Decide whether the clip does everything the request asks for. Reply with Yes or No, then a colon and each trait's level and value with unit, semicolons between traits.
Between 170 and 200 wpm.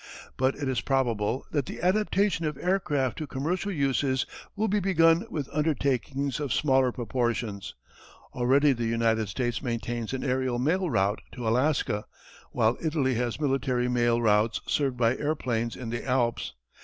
No: average, 155 wpm